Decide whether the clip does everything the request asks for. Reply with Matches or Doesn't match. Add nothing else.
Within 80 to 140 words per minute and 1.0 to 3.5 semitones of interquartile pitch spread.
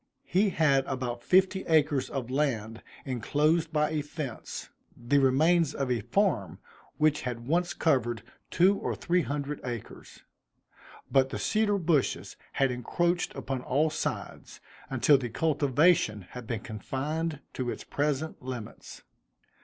Doesn't match